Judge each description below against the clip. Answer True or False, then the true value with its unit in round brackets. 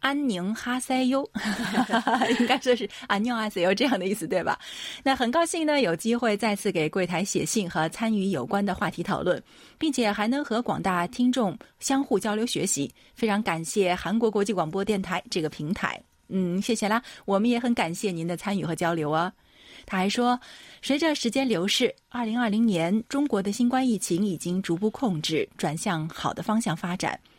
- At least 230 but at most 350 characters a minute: True (285 characters per minute)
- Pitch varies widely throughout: False (4.7 semitones)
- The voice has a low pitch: False (210 Hz)